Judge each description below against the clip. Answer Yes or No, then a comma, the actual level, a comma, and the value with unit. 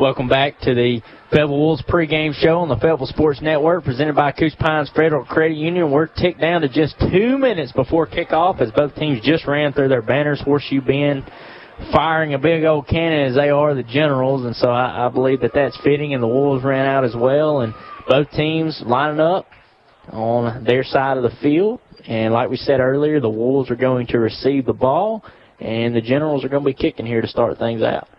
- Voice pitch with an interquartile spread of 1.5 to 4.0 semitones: Yes, average, 3.3 semitones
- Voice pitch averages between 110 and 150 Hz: Yes, medium, 140 Hz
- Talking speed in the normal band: No, fast, 215 wpm